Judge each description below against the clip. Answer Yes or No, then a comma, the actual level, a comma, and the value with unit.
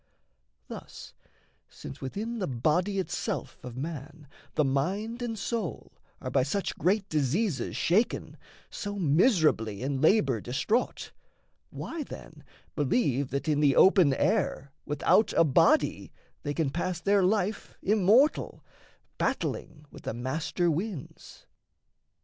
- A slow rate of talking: Yes, slow, 120 wpm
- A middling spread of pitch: No, wide, 6.7 semitones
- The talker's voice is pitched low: No, medium, 165 Hz